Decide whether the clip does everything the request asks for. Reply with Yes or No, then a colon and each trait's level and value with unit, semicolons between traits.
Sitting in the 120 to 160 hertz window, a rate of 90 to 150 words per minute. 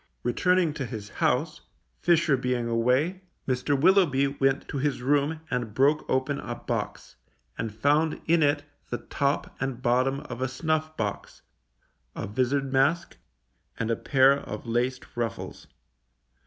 Yes: low, 135 Hz; average, 140 wpm